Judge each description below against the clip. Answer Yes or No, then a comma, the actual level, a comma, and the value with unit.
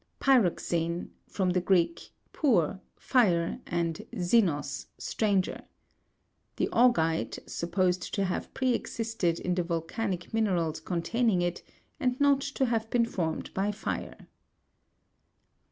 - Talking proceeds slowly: Yes, slow, 115 wpm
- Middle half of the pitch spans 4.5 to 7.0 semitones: Yes, average, 5.1 semitones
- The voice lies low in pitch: No, medium, 185 Hz